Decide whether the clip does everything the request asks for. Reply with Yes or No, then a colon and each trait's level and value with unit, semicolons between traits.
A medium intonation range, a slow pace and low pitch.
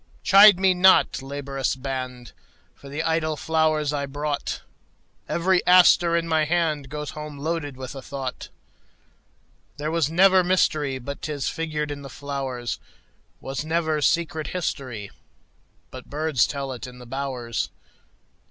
No: average, 3.2 semitones; slow, 115 wpm; medium, 150 Hz